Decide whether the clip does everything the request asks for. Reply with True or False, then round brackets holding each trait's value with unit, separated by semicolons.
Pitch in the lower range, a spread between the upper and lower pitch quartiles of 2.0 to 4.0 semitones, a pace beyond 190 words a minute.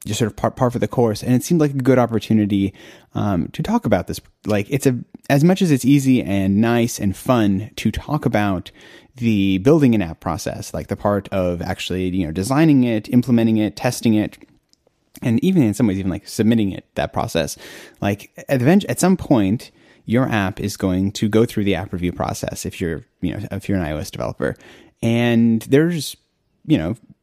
False (110 Hz; 4.5 semitones; 205 wpm)